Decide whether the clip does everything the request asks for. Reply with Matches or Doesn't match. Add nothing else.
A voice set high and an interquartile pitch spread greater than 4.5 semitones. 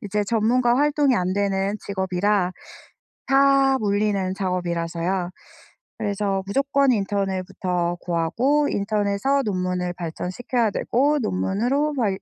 Matches